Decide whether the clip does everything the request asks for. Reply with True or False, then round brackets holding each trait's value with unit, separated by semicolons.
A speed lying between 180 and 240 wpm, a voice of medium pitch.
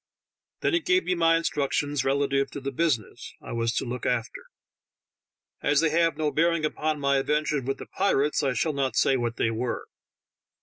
True (185 wpm; 145 Hz)